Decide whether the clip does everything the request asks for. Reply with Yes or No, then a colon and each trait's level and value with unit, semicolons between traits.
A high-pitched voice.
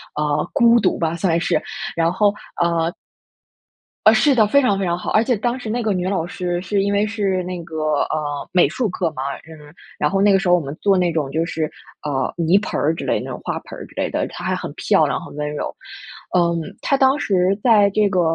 No: medium, 180 Hz